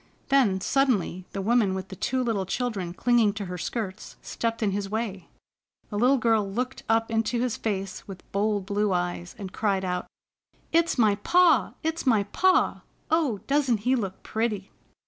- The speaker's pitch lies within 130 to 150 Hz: No, high, 215 Hz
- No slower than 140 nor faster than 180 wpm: Yes, average, 170 wpm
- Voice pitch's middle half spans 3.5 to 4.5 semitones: Yes, average, 4.1 semitones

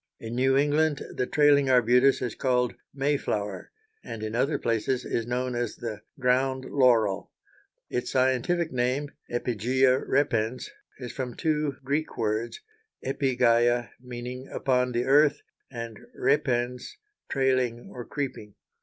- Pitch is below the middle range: Yes, low, 125 Hz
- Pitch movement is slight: Yes, narrow, 2.2 semitones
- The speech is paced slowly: Yes, slow, 125 wpm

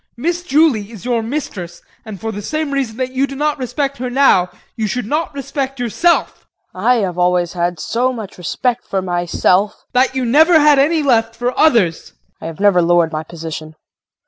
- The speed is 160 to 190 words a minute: No, average, 200 wpm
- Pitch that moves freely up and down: Yes, wide, 7.2 semitones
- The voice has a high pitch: Yes, high, 235 Hz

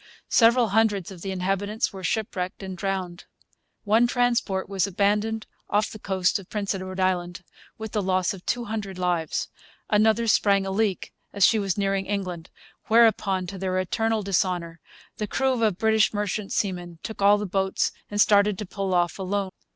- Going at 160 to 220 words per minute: Yes, average, 175 wpm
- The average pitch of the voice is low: No, high, 195 Hz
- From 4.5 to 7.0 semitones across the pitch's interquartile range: No, narrow, 2.5 semitones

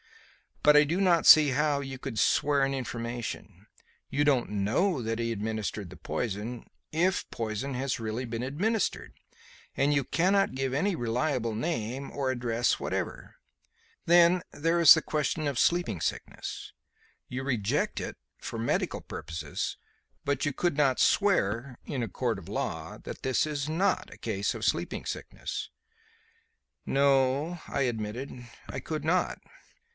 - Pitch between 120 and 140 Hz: Yes, low, 135 Hz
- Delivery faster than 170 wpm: No, average, 150 wpm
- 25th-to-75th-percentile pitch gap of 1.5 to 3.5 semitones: No, average, 4.8 semitones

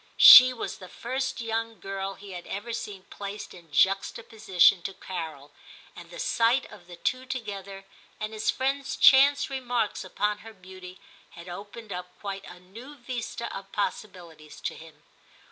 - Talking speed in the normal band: Yes, average, 160 wpm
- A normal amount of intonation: Yes, average, 4.4 semitones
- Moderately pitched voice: No, high, 200 Hz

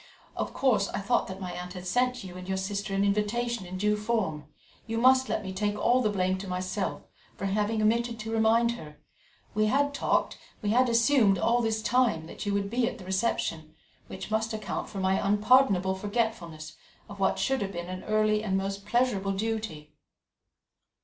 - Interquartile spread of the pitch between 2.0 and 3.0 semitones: No, average, 3.4 semitones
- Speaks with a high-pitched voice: Yes, high, 205 Hz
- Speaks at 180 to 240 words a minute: Yes, average, 195 wpm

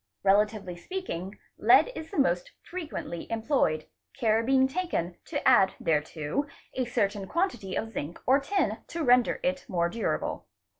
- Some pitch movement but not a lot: No, wide, 7.1 semitones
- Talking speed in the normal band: Yes, average, 145 wpm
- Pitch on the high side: Yes, high, 225 Hz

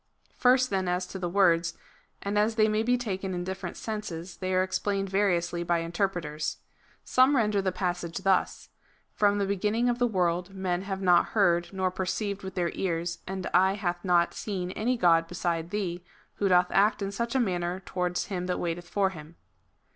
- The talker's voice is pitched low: No, high, 190 Hz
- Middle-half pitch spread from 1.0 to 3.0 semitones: Yes, narrow, 2.6 semitones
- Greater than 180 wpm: Yes, average, 190 wpm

